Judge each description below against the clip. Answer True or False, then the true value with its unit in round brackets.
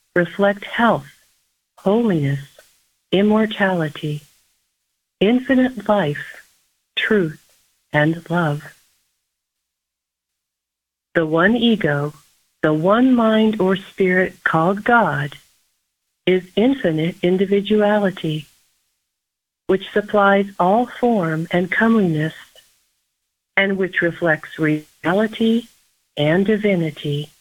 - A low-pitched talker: False (180 Hz)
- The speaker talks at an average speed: False (75 wpm)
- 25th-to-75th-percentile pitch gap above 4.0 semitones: True (5.3 semitones)